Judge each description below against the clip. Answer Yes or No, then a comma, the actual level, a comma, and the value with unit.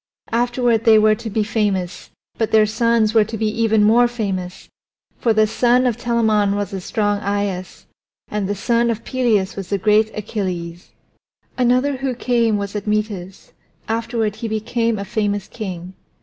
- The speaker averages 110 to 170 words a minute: Yes, average, 155 wpm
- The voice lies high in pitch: Yes, high, 215 Hz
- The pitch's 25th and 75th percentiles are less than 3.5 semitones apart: Yes, narrow, 2.4 semitones